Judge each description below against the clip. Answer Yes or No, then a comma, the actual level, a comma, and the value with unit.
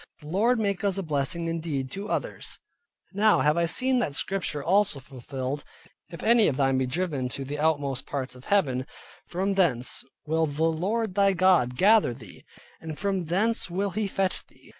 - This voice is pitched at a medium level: Yes, medium, 165 Hz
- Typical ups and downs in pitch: No, wide, 6.0 semitones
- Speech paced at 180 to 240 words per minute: Yes, average, 190 wpm